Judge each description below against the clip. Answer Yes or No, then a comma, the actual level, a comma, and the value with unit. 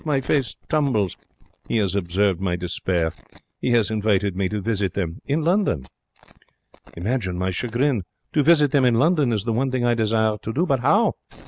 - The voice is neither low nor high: No, low, 110 Hz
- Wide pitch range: Yes, wide, 5.9 semitones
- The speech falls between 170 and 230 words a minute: Yes, average, 185 wpm